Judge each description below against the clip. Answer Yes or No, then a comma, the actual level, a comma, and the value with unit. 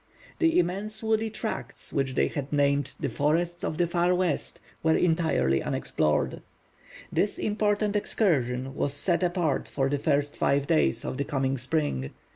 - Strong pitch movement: No, average, 5.0 semitones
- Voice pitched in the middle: Yes, medium, 155 Hz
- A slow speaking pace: No, average, 155 wpm